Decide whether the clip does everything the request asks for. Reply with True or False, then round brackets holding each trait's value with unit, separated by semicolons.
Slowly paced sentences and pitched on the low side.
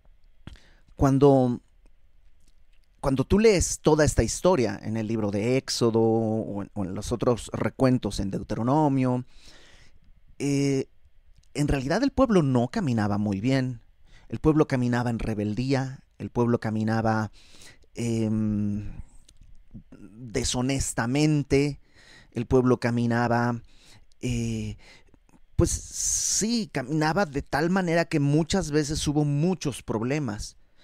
True (110 wpm; 120 Hz)